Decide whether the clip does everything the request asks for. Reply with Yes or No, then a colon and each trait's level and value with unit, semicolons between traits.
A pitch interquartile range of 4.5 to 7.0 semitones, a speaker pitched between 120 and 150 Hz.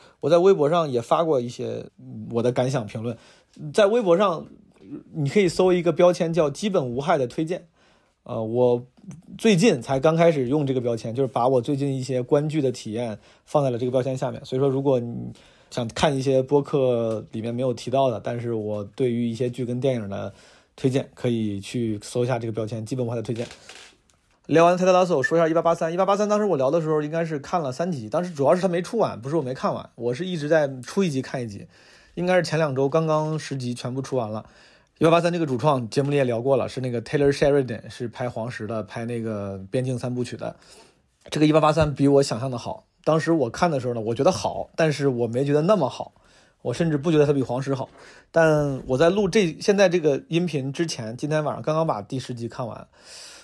Yes: average, 5.1 semitones; low, 135 Hz